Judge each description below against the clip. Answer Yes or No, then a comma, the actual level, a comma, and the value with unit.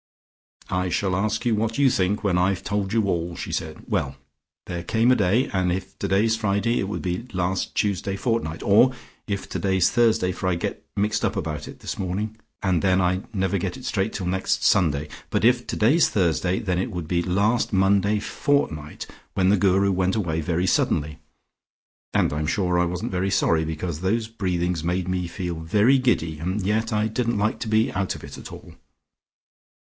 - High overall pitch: No, very low, 95 Hz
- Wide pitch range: No, average, 3.4 semitones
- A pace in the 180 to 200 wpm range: Yes, average, 190 wpm